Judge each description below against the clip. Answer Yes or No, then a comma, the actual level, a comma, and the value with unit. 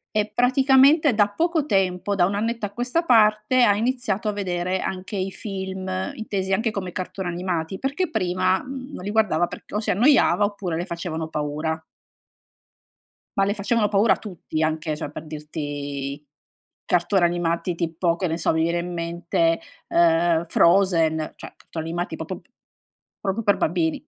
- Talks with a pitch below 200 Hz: Yes, medium, 185 Hz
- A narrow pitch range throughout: No, average, 4.0 semitones